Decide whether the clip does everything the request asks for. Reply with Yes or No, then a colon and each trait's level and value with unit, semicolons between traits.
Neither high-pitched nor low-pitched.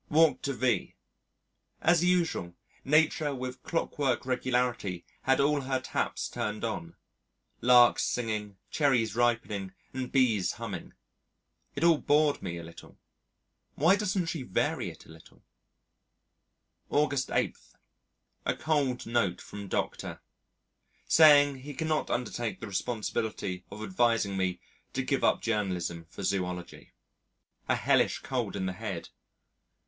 No: low, 120 Hz